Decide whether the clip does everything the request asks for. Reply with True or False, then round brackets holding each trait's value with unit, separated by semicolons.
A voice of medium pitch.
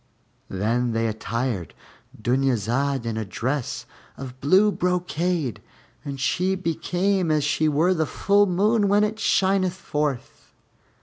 True (150 Hz)